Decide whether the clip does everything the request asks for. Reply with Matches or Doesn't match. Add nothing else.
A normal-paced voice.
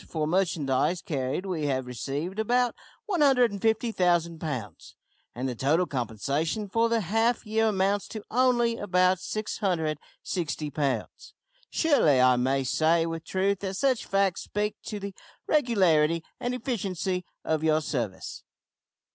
Doesn't match